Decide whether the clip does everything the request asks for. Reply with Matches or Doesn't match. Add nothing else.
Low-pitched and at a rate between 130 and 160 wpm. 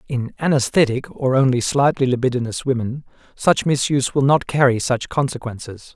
Matches